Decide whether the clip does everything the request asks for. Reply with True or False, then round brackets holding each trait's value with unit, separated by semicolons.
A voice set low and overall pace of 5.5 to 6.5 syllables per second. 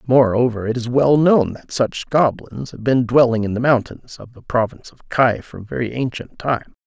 False (120 Hz; 4.8 syllables/s)